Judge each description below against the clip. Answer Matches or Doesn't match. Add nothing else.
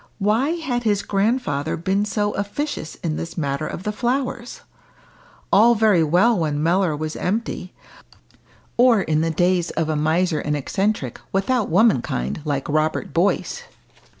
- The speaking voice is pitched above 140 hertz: Matches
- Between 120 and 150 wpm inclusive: Matches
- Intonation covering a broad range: Matches